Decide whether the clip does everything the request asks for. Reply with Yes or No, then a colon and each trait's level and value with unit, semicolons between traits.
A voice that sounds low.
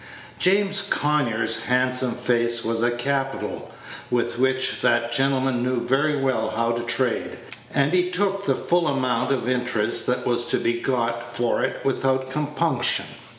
Yes: low, 125 Hz